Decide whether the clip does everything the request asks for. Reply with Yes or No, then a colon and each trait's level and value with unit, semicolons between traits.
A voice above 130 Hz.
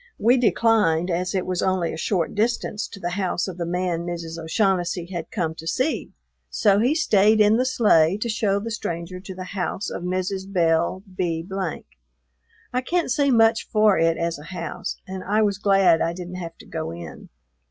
Yes: medium, 185 Hz